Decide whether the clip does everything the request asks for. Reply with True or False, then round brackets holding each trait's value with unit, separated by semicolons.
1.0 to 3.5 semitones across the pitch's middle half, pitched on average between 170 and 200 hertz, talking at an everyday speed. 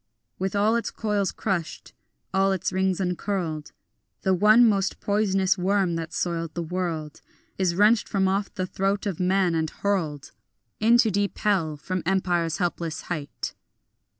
True (2.9 semitones; 190 Hz; 150 wpm)